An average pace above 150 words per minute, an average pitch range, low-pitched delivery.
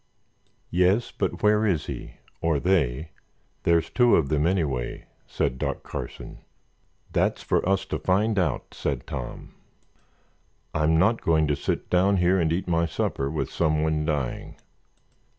No: average, 140 wpm; average, 3.7 semitones; very low, 85 Hz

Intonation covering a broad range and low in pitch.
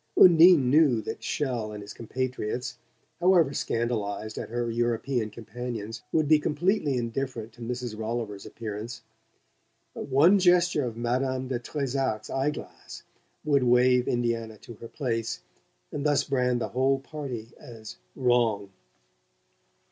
No: average, 3.2 semitones; low, 125 Hz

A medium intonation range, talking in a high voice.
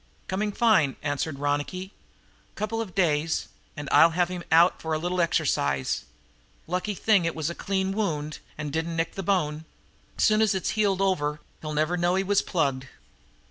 No: average, 4.2 semitones; medium, 170 Hz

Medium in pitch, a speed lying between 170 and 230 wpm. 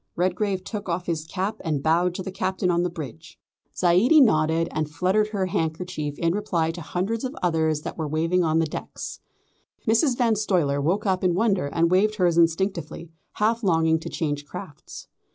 Yes: medium, 175 Hz; average, 185 wpm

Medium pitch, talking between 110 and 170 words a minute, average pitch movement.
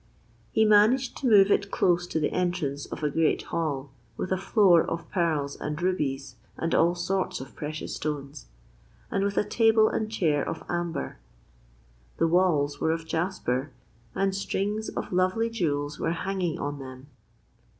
Yes: medium, 170 Hz; average, 160 wpm; average, 4.8 semitones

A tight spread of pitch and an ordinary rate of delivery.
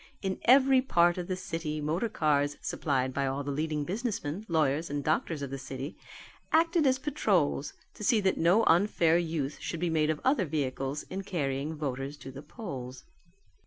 No: average, 5.2 semitones; average, 180 wpm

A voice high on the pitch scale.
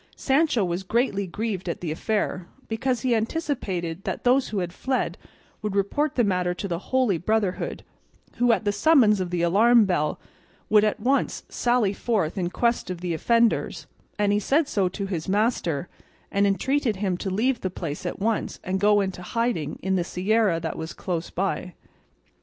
Yes: high, 200 Hz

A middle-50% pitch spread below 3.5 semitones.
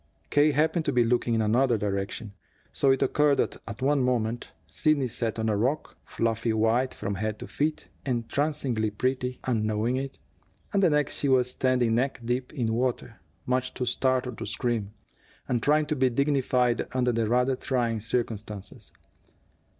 Yes: average, 2.9 semitones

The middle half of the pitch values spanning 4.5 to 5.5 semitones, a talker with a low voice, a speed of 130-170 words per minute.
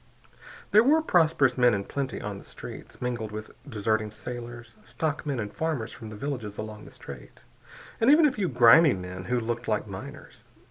No: average, 5.2 semitones; low, 120 Hz; average, 180 wpm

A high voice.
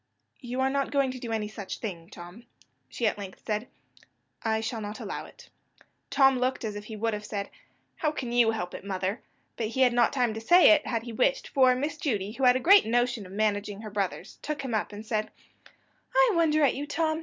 Yes: high, 230 Hz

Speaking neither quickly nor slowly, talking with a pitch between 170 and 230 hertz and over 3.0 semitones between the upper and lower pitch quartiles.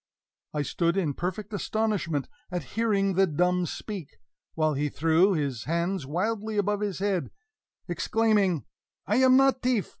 Yes: average, 145 wpm; high, 190 Hz; average, 4.3 semitones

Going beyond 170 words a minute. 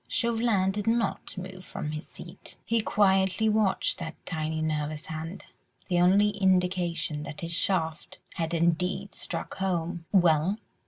No: average, 140 wpm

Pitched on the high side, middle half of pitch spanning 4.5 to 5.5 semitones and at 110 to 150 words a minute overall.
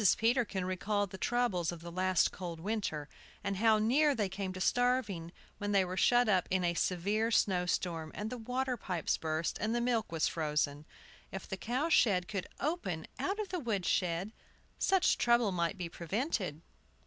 No: high, 195 Hz; average, 5.2 semitones; average, 185 wpm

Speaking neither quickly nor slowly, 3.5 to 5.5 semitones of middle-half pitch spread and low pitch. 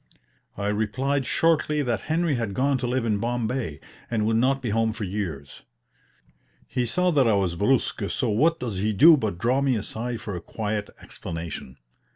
Yes: average, 185 wpm; average, 4.5 semitones; low, 115 Hz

